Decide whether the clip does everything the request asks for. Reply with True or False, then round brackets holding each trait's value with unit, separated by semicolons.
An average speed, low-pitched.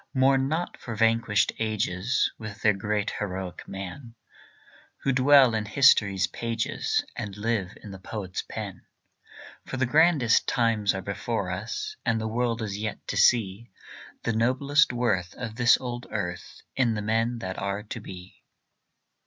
True (155 wpm; 110 Hz)